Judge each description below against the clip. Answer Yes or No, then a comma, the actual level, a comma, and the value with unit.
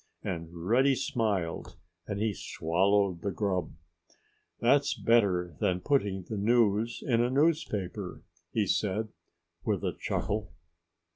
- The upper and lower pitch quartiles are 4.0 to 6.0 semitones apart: Yes, average, 4.3 semitones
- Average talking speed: No, slow, 120 wpm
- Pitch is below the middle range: Yes, low, 105 Hz